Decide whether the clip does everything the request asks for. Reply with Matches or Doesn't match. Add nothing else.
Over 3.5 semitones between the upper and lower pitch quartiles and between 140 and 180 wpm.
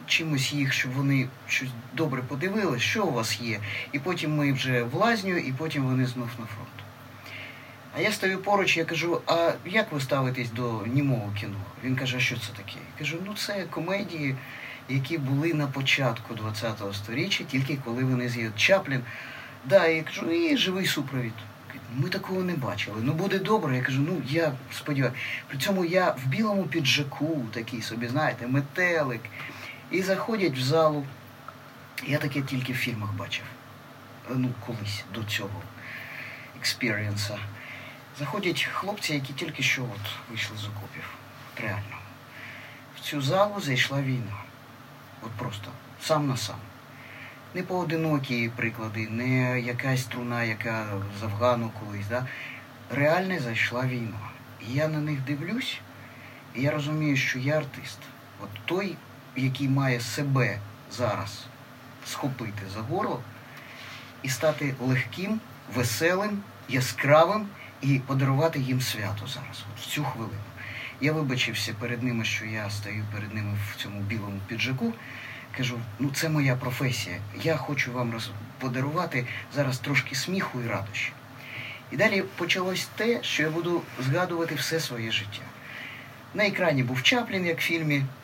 Matches